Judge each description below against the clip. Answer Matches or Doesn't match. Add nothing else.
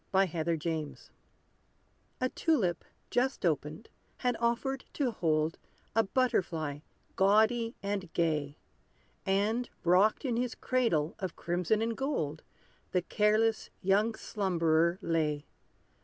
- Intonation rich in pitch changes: Matches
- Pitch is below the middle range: Doesn't match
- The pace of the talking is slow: Matches